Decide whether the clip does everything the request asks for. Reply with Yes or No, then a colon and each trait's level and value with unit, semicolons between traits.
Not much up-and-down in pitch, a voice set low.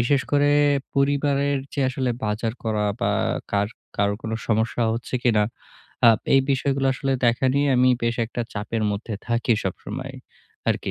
No: average, 3.8 semitones; low, 120 Hz